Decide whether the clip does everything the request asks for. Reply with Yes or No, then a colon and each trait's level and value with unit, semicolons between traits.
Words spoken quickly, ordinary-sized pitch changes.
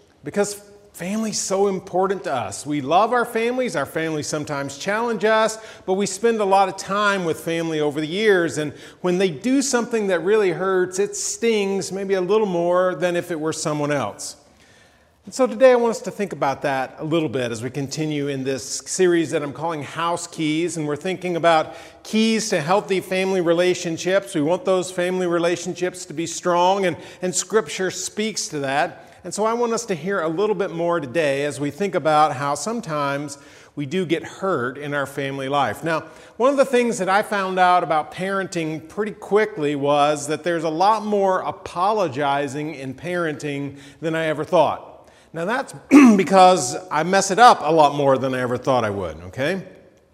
No: average, 195 wpm; average, 4.6 semitones